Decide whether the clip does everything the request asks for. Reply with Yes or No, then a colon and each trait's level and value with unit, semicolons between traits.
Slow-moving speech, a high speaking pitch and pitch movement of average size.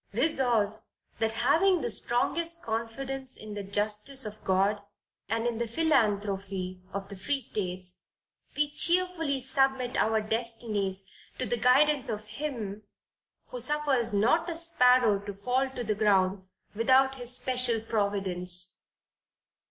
Yes: slow, 130 wpm; high, 230 Hz; average, 4.7 semitones